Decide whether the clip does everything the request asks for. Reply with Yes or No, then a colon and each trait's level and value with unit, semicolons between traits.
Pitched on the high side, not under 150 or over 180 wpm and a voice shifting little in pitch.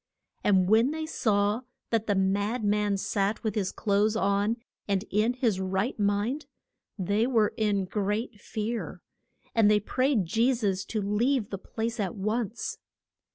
Yes: high, 210 Hz; average, 155 wpm; narrow, 2.3 semitones